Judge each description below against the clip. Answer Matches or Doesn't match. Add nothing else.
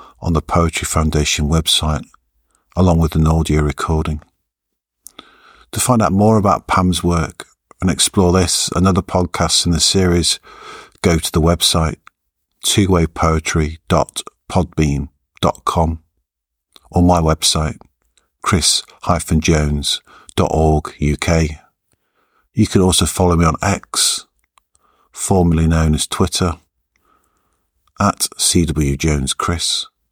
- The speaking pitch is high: Doesn't match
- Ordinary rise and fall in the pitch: Doesn't match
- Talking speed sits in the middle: Doesn't match